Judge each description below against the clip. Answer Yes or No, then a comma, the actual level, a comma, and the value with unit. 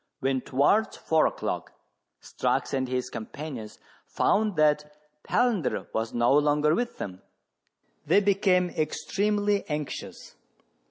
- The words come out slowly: Yes, slow, 110 wpm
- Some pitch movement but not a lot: No, wide, 7.1 semitones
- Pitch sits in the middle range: Yes, medium, 150 Hz